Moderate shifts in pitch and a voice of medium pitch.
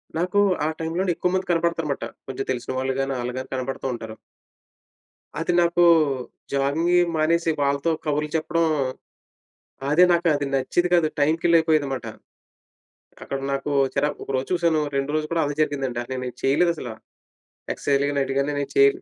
Yes: average, 3.7 semitones; medium, 145 Hz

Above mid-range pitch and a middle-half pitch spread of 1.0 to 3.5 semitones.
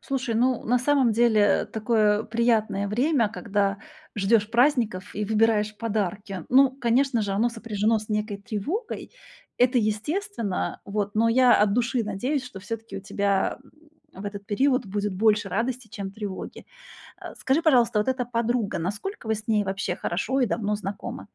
Yes: high, 220 Hz; average, 3.1 semitones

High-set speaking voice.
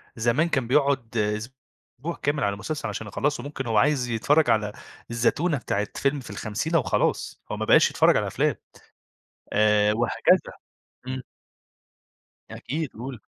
No: low, 125 Hz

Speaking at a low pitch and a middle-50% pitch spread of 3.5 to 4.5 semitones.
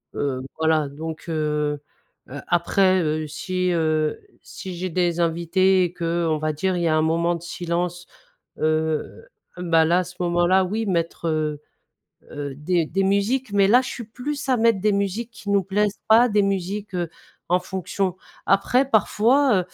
No: medium, 180 Hz; average, 3.8 semitones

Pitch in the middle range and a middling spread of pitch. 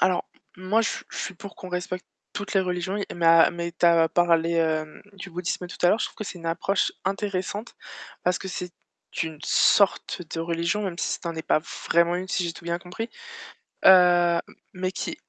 No: medium, 180 Hz; narrow, 2.0 semitones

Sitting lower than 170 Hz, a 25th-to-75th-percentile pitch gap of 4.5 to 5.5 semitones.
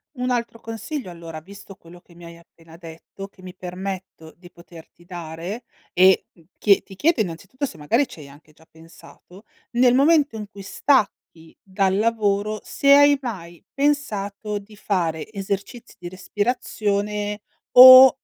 No: high, 200 Hz; average, 4.9 semitones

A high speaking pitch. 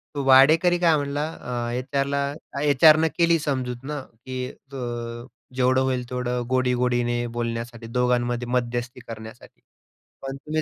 No: low, 125 Hz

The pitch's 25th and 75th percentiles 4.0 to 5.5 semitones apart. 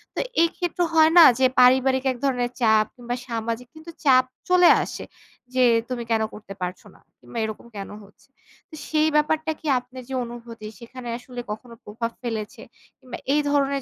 No: average, 3.5 semitones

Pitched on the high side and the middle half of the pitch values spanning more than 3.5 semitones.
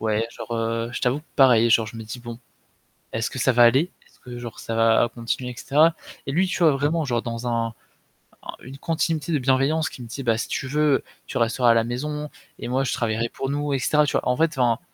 No: low, 125 Hz; average, 3.9 semitones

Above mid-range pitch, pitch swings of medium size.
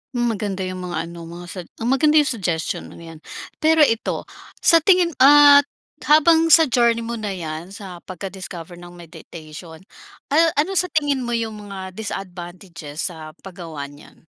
No: high, 195 Hz; wide, 7.9 semitones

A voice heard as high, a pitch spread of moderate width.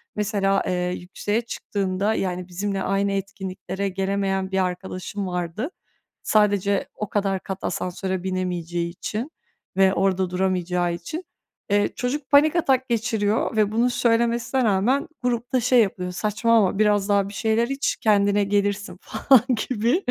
Yes: high, 200 Hz; average, 3.2 semitones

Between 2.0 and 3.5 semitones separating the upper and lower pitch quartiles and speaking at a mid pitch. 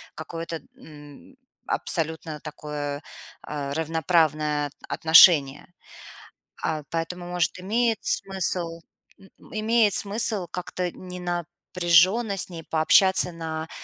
Yes: average, 2.9 semitones; medium, 165 Hz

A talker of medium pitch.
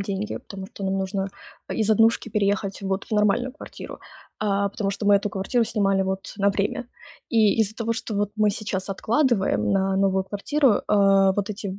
No: high, 200 Hz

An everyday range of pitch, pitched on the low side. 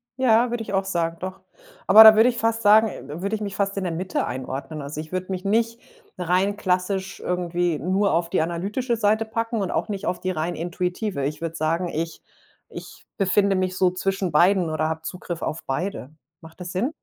No: average, 3.6 semitones; medium, 185 Hz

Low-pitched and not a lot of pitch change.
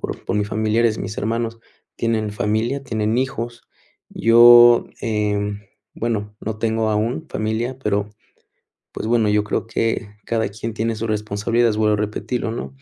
Yes: low, 110 Hz; narrow, 1.7 semitones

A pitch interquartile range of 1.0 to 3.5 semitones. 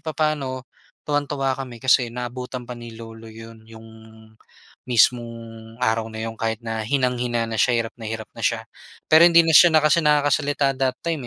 No: average, 3.9 semitones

